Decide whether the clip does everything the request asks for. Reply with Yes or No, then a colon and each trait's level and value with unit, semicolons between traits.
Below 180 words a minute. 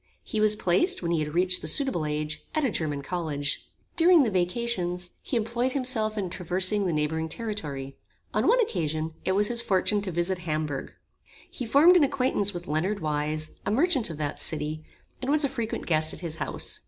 No: average, 195 wpm